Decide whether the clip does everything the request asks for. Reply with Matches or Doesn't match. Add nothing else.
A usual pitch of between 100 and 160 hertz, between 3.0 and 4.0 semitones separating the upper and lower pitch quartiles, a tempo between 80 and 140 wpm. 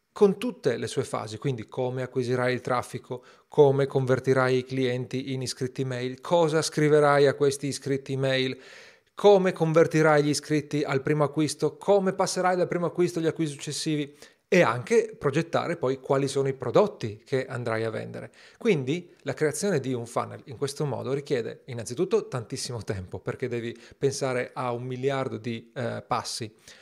Doesn't match